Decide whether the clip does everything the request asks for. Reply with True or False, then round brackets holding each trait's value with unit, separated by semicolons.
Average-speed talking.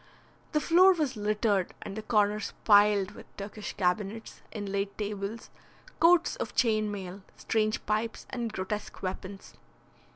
False (130 wpm)